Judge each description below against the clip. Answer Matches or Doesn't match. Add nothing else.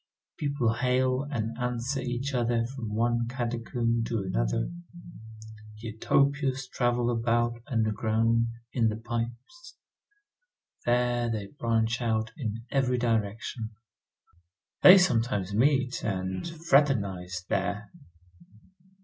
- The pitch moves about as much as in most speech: Doesn't match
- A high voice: Doesn't match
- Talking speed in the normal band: Doesn't match